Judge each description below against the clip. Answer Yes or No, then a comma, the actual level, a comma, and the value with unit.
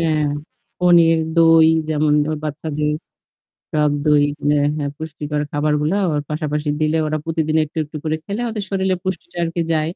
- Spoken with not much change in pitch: Yes, narrow, 1.7 semitones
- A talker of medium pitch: Yes, medium, 155 Hz